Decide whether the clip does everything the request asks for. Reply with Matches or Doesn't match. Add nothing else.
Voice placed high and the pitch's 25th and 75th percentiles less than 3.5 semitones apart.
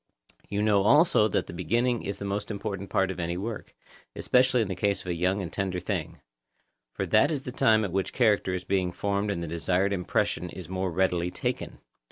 Doesn't match